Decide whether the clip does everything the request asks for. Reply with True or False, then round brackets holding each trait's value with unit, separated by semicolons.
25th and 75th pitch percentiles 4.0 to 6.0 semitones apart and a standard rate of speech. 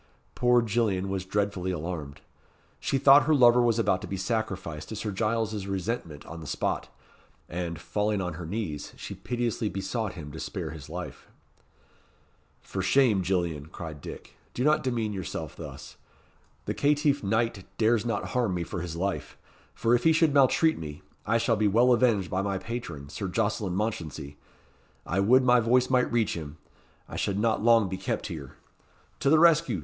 True (5.0 semitones; 175 wpm)